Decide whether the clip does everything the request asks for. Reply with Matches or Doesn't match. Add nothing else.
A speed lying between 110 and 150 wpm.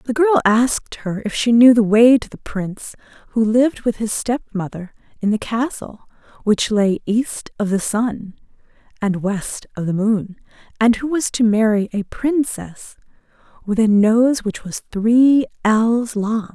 Doesn't match